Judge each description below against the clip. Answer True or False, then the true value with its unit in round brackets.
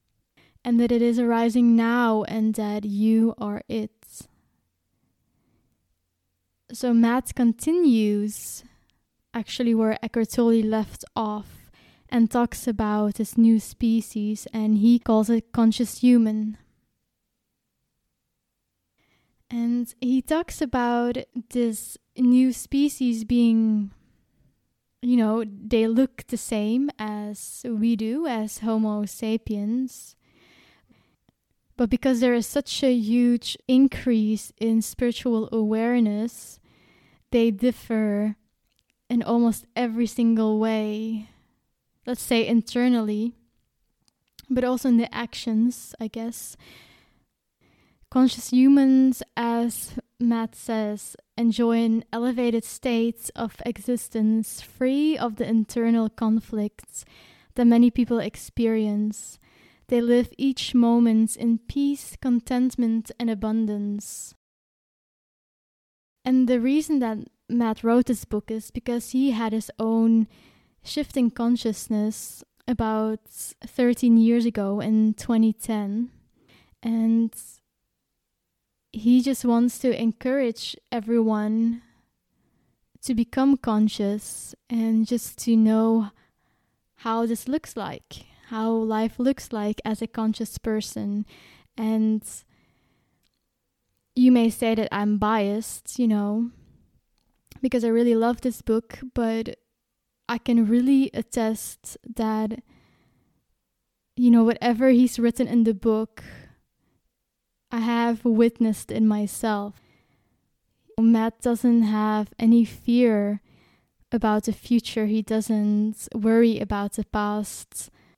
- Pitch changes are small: True (1.7 semitones)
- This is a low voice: False (230 Hz)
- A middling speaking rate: False (105 wpm)